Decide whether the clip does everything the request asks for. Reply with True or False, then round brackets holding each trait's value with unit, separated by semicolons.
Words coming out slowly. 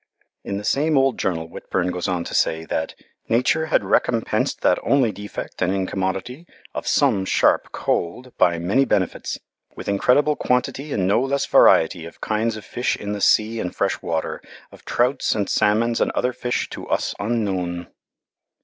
False (170 wpm)